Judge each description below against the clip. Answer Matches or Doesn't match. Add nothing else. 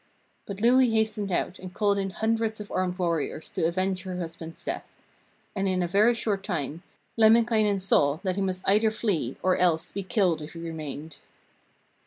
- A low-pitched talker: Doesn't match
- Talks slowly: Doesn't match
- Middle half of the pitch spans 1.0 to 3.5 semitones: Doesn't match